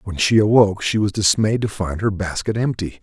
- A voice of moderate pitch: No, low, 100 Hz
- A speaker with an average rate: No, fast, 220 wpm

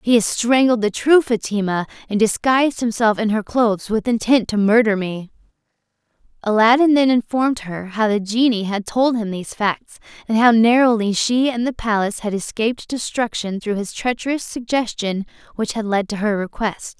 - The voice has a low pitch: No, high, 225 Hz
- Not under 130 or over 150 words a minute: No, average, 175 wpm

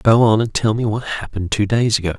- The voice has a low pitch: Yes, low, 110 Hz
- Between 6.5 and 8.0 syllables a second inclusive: Yes, 6.7 syllables/s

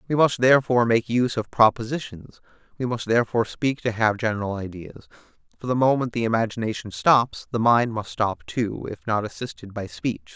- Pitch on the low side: Yes, low, 115 Hz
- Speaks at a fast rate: No, average, 180 wpm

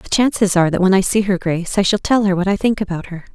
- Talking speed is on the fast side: Yes, fast, 325 wpm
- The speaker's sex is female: Yes, female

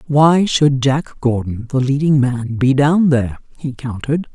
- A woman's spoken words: Yes, female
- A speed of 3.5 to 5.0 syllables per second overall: Yes, 4.5 syllables/s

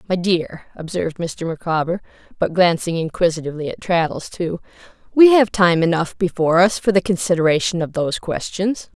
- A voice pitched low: No, medium, 175 Hz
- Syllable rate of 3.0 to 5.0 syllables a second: No, 5.5 syllables/s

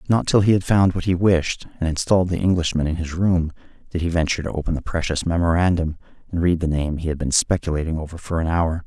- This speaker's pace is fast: Yes, fast, 235 wpm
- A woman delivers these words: No, male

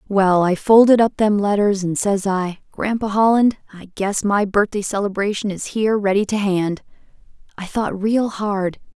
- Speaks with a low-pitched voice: No, high, 205 Hz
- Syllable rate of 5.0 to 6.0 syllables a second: No, 4.6 syllables/s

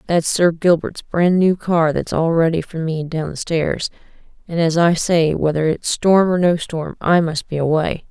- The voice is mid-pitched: Yes, medium, 165 Hz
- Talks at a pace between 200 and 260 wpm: Yes, fast, 205 wpm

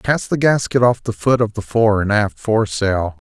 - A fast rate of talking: Yes, fast, 220 wpm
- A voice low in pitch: Yes, low, 110 Hz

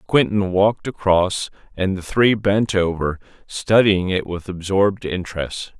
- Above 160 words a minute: No, slow, 135 wpm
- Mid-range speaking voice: No, very low, 95 Hz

